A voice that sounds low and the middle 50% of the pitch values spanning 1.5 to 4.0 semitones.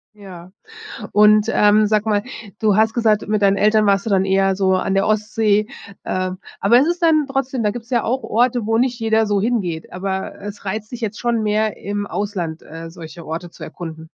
No: high, 210 Hz; narrow, 2.6 semitones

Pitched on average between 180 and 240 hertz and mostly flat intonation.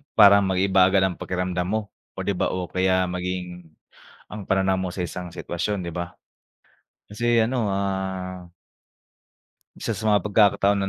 No: very low, 95 Hz; narrow, 1.8 semitones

